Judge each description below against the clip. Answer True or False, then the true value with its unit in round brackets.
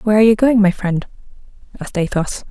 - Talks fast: False (190 wpm)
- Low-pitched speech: False (205 Hz)